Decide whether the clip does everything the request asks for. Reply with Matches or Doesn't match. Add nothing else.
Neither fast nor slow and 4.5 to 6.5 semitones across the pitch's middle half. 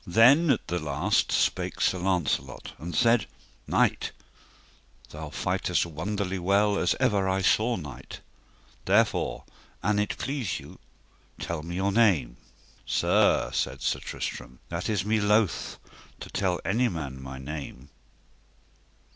Doesn't match